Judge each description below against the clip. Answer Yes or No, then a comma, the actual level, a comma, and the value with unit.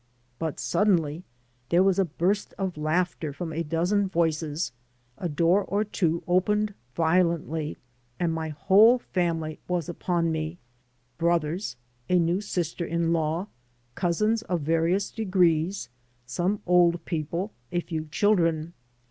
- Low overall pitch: No, medium, 170 Hz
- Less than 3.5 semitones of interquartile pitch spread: Yes, narrow, 2.6 semitones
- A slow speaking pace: Yes, slow, 130 wpm